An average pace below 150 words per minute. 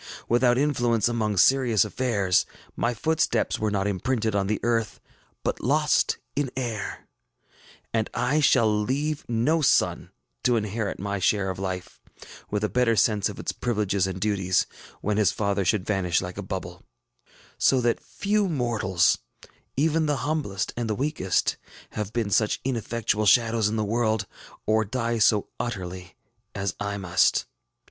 No: average, 155 wpm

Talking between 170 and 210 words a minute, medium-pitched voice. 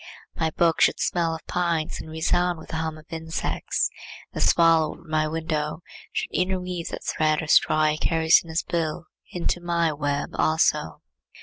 Yes: average, 175 wpm; medium, 160 Hz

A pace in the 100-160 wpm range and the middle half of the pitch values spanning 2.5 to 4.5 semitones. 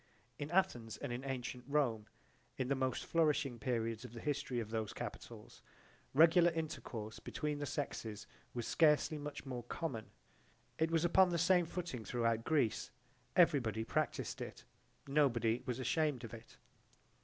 No: average, 150 wpm; average, 5.0 semitones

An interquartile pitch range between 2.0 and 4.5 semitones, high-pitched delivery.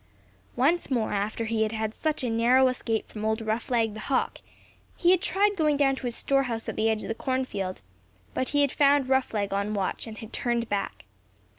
Yes: average, 3.8 semitones; high, 235 Hz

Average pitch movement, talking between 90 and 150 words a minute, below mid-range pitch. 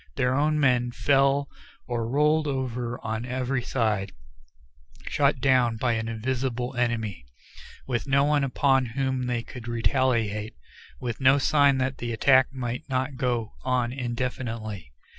No: narrow, 2.3 semitones; average, 140 wpm; low, 125 Hz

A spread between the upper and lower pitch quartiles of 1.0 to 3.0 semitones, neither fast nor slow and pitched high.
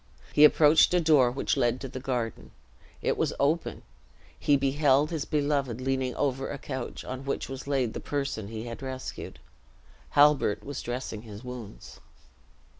No: average, 2.7 semitones; average, 160 wpm; low, 135 Hz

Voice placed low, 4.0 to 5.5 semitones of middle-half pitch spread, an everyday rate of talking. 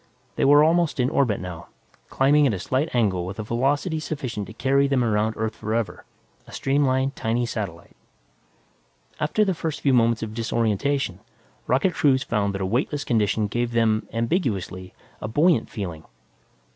Yes: low, 120 Hz; average, 4.6 semitones; average, 160 wpm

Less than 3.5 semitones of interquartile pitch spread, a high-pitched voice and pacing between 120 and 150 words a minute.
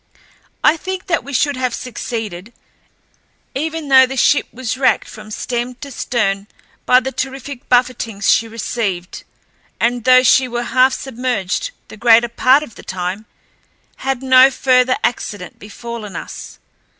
Yes: average, 2.8 semitones; very high, 250 Hz; average, 145 wpm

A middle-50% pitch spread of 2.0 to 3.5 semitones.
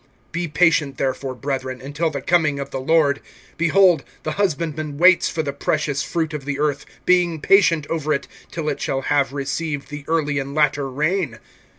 Yes: average, 2.9 semitones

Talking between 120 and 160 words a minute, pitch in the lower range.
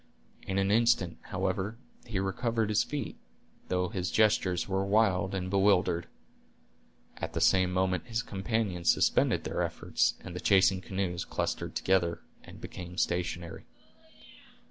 Yes: slow, 135 wpm; very low, 95 Hz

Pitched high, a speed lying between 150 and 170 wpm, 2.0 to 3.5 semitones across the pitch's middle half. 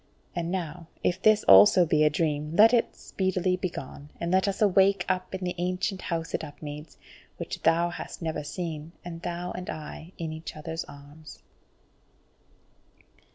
No: medium, 170 Hz; average, 160 wpm; average, 3.0 semitones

